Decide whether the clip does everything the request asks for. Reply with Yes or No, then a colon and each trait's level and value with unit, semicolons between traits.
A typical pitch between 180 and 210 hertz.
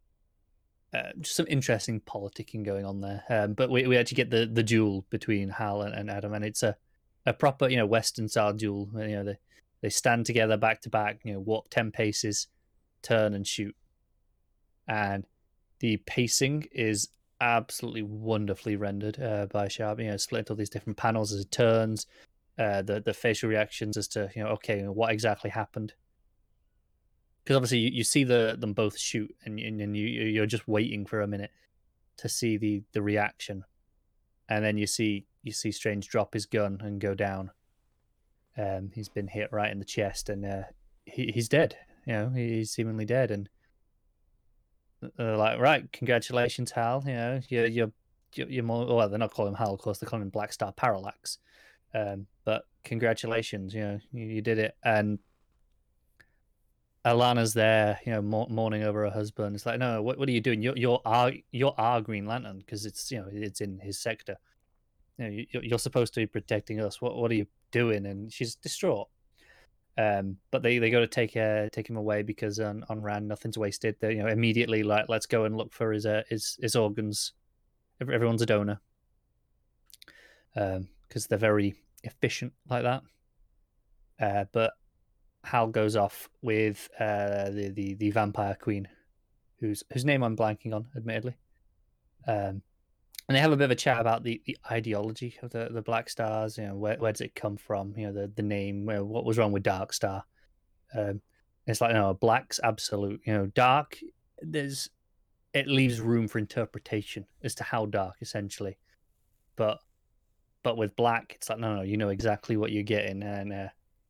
No: low, 110 Hz